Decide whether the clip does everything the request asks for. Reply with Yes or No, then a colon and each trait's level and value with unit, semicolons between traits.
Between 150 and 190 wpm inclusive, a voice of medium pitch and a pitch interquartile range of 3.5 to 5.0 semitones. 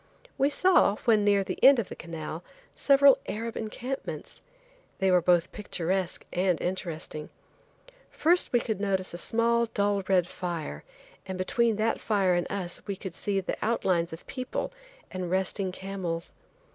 No: average, 155 wpm; high, 195 Hz; average, 4.1 semitones